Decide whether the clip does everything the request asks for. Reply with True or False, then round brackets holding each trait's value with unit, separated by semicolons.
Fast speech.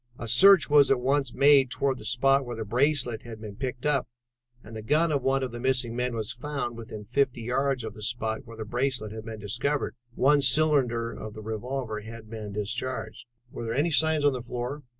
True (215 wpm)